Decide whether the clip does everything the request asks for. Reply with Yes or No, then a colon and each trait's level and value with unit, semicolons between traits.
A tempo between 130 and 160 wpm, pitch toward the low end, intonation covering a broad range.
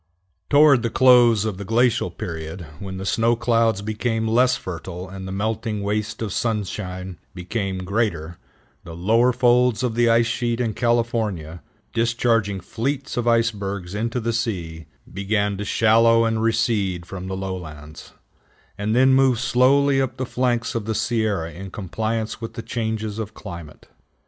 No: average, 155 wpm; low, 110 Hz; average, 3.6 semitones